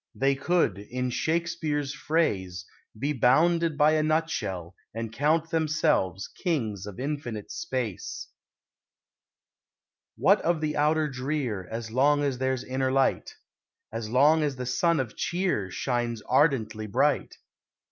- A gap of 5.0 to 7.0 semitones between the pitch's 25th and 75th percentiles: Yes, average, 5.3 semitones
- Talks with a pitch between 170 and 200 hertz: No, low, 135 Hz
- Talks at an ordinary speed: No, slow, 130 wpm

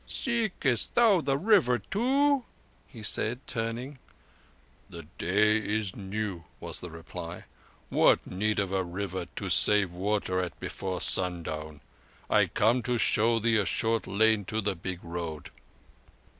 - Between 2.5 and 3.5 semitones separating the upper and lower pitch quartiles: No, average, 4.8 semitones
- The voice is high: No, low, 105 Hz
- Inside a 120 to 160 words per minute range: Yes, average, 140 wpm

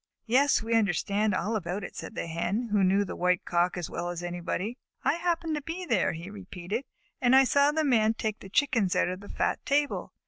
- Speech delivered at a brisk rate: Yes, fast, 220 wpm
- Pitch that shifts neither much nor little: No, wide, 6.5 semitones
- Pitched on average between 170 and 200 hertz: No, high, 210 Hz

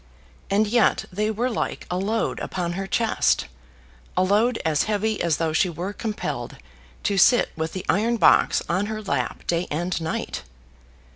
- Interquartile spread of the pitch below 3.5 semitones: No, average, 4.0 semitones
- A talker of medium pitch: No, high, 195 Hz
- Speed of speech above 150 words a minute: Yes, average, 165 wpm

